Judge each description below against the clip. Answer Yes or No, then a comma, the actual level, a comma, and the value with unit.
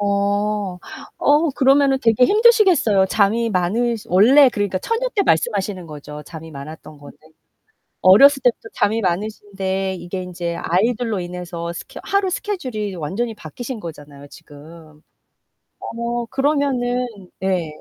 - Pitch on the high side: Yes, high, 205 Hz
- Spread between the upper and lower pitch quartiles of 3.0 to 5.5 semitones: No, wide, 5.9 semitones